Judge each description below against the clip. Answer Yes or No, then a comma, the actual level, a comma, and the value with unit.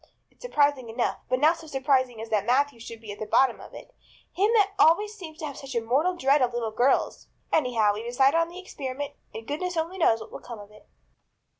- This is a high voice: Yes, very high, 270 Hz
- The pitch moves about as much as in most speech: No, wide, 5.7 semitones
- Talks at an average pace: No, fast, 235 wpm